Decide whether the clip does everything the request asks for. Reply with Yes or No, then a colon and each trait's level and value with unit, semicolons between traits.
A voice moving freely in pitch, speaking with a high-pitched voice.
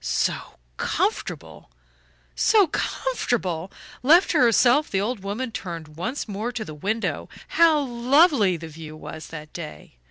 Yes: wide, 7.9 semitones; high, 220 Hz